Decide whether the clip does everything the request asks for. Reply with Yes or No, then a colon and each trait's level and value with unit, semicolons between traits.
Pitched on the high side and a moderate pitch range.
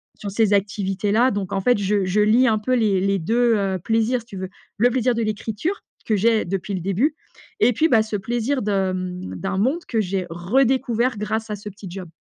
Yes: high, 210 Hz; average, 3.3 semitones